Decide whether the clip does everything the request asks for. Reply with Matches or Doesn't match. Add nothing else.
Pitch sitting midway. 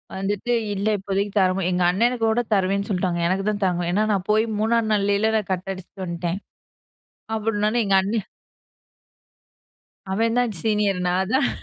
Doesn't match